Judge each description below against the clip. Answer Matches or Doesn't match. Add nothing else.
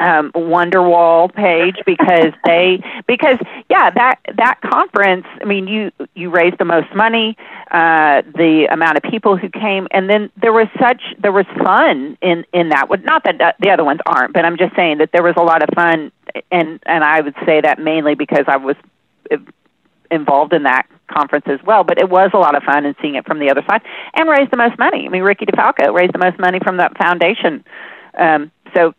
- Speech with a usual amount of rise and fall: Matches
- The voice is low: Doesn't match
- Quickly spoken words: Matches